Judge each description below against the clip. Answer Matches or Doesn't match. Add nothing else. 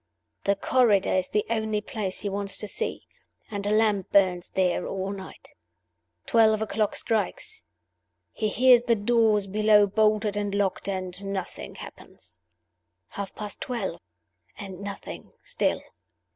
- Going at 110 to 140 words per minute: Matches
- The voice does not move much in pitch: Matches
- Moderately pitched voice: Doesn't match